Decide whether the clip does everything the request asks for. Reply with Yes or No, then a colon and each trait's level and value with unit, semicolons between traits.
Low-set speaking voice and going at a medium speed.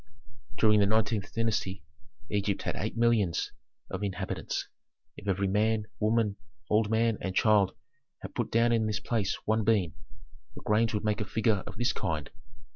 Yes: low, 105 Hz; average, 165 wpm